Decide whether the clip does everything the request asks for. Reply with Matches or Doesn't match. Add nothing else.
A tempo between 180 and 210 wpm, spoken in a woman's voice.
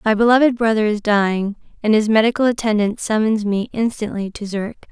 Doesn't match